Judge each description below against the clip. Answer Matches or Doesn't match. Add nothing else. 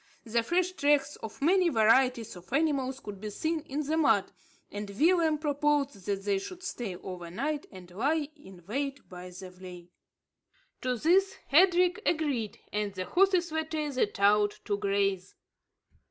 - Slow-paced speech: Doesn't match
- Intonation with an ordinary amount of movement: Doesn't match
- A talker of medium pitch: Doesn't match